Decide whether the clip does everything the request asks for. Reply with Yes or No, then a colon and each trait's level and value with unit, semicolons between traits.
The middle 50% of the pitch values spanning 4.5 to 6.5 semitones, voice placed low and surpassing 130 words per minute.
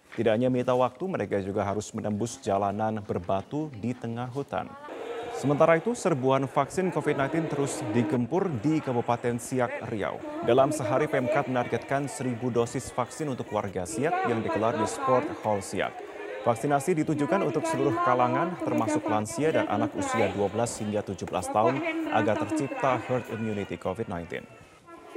Yes: wide, 5.4 semitones; low, 125 Hz; fast, 140 wpm